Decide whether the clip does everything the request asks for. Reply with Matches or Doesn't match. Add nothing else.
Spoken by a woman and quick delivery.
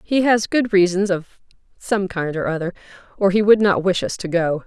Matches